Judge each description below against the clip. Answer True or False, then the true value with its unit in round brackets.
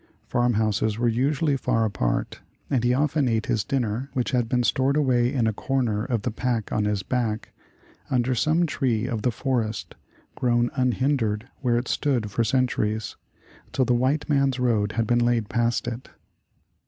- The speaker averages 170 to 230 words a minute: True (175 wpm)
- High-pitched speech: False (120 Hz)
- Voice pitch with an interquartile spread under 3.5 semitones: True (2.8 semitones)